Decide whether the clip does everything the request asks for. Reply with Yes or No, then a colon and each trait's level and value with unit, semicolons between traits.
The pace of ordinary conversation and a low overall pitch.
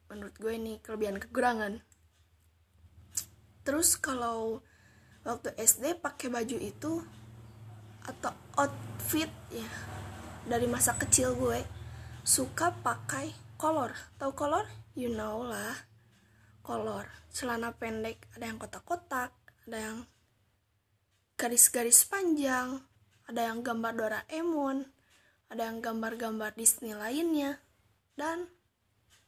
No: average, 95 wpm; high, 225 Hz